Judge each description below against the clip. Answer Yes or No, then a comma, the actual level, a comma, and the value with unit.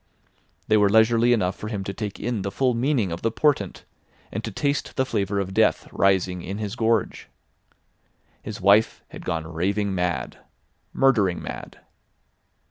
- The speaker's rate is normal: Yes, average, 155 wpm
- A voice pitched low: Yes, low, 105 Hz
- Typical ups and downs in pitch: Yes, average, 3.2 semitones